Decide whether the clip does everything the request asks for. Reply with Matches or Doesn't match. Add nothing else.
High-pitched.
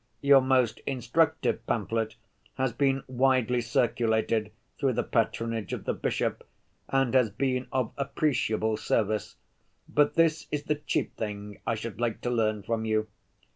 Doesn't match